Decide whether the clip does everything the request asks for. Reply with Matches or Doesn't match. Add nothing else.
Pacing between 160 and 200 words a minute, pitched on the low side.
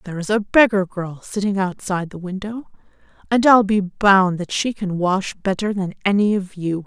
Doesn't match